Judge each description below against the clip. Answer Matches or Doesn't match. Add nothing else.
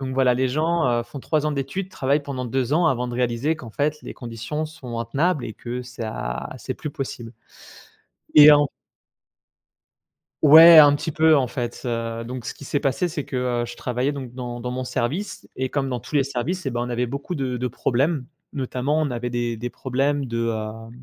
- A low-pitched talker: Matches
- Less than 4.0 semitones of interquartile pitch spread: Matches